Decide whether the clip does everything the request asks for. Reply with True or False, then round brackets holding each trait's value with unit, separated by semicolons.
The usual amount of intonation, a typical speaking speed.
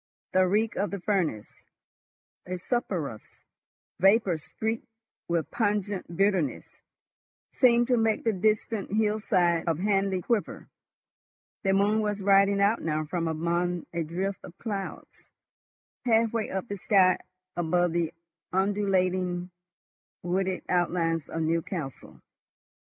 False (3.3 semitones; 115 wpm)